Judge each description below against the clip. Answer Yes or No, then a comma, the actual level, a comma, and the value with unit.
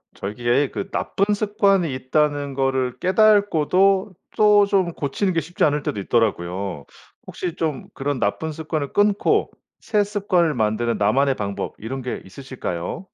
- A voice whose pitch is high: No, medium, 150 Hz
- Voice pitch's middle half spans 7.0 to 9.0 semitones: Yes, wide, 7.7 semitones